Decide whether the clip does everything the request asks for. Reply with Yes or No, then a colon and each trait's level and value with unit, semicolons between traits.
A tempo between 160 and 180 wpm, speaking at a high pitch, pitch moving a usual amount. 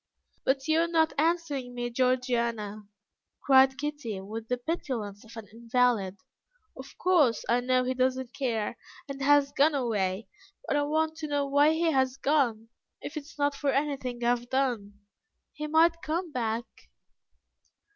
Yes: average, 165 wpm; very high, 260 Hz; average, 3.9 semitones